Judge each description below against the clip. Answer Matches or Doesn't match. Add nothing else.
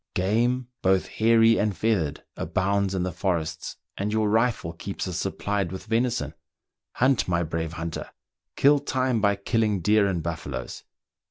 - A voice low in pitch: Matches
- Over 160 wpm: Doesn't match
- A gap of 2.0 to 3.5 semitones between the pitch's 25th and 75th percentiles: Doesn't match